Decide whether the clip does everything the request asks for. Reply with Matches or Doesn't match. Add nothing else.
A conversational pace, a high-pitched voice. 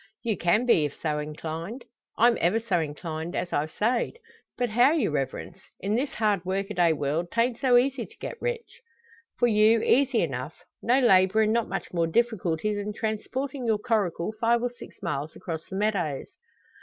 Matches